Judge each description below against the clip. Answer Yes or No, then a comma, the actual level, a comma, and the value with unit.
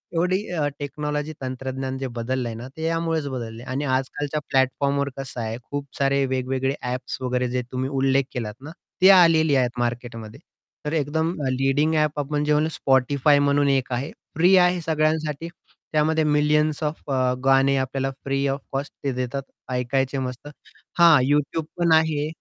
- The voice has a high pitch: No, medium, 140 Hz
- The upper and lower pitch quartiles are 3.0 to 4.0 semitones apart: No, narrow, 2.6 semitones